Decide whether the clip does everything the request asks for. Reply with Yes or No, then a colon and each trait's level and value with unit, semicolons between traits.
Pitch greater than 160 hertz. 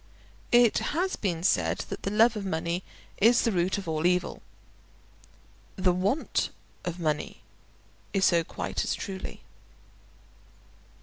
Yes: medium, 185 Hz